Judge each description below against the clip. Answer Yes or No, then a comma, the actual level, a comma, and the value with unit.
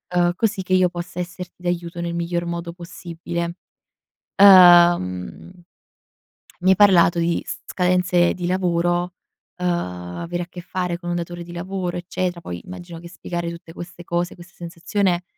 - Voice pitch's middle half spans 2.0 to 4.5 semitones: No, narrow, 0.9 semitones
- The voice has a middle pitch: Yes, medium, 175 Hz